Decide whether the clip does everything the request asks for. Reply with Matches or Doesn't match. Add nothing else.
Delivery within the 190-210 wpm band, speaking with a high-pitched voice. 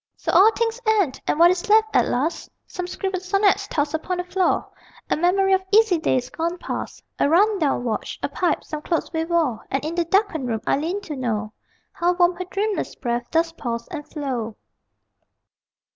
Matches